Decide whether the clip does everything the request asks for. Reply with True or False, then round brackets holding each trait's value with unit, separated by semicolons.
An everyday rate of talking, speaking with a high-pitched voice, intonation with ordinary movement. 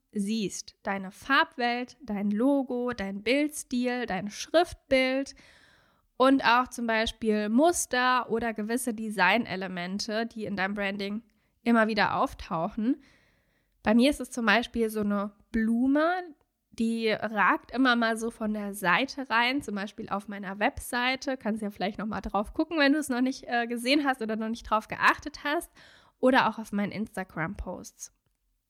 True (155 wpm; 230 Hz; 3.8 semitones)